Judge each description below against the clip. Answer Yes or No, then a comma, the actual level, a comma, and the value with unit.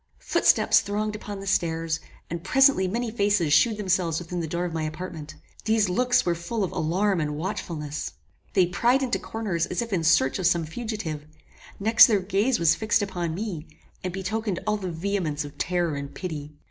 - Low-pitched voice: No, medium, 180 Hz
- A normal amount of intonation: Yes, average, 4.3 semitones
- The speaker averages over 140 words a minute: Yes, average, 185 wpm